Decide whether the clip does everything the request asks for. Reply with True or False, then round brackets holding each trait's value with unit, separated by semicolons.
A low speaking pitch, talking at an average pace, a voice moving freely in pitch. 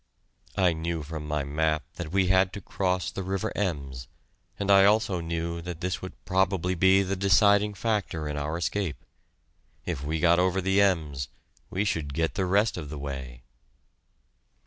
False (90 Hz; 170 wpm; 3.9 semitones)